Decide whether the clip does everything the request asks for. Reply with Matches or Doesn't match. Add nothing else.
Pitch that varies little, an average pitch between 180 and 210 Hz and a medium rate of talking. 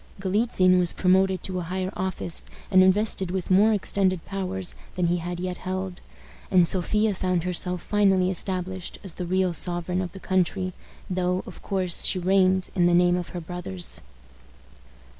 Matches